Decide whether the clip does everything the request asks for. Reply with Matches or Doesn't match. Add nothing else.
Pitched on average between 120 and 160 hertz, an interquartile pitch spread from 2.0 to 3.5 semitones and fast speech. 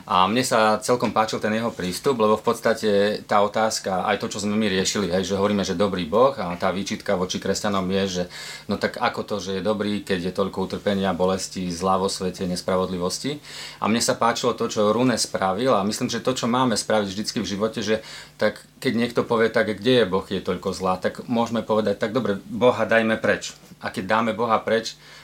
Doesn't match